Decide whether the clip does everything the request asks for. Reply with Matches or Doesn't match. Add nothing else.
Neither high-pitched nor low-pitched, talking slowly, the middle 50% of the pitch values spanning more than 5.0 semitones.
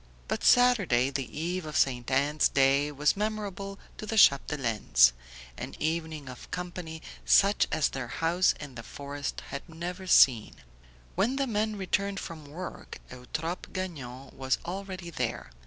Doesn't match